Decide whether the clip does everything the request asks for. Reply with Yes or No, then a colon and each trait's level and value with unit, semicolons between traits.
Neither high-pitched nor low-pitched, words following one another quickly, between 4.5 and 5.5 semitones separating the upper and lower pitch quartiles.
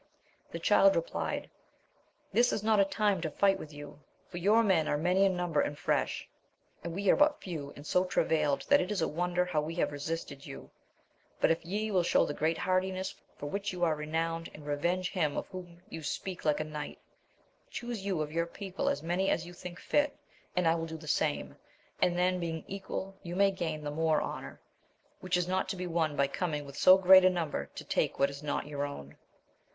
No: medium, 175 Hz; fast, 220 wpm; average, 3.6 semitones